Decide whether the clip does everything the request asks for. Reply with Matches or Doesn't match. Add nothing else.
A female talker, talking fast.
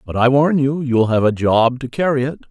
Doesn't match